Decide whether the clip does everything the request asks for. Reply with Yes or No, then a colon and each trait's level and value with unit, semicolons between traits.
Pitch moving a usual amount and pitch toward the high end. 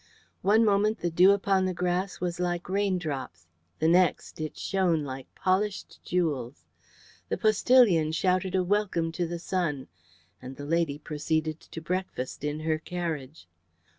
No: average, 3.3 semitones; medium, 175 Hz